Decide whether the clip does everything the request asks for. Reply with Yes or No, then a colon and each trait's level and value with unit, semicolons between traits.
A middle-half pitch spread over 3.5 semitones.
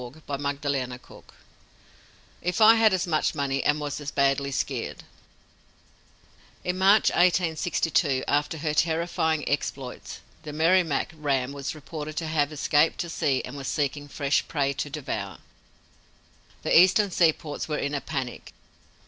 No: average, 2.7 semitones